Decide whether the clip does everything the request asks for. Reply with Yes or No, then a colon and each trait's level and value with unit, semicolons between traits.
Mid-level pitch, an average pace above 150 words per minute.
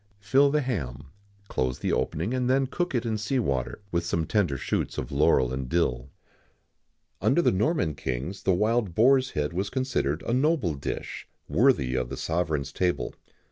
No: very low, 95 Hz; average, 180 wpm